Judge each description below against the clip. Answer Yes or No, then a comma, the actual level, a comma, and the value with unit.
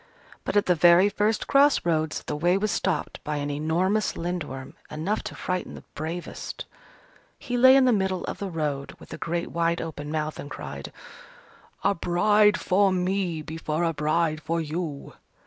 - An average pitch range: Yes, average, 3.9 semitones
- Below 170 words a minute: No, average, 175 wpm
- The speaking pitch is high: No, medium, 170 Hz